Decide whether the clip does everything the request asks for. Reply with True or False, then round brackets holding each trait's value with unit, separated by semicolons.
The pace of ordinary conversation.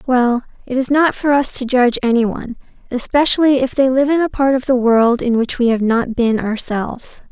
False (215 wpm)